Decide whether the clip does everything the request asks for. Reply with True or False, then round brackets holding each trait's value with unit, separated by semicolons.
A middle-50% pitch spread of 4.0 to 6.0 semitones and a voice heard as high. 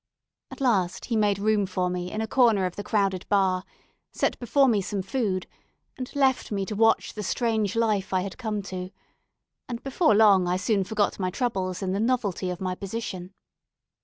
False (3.3 semitones; 200 Hz)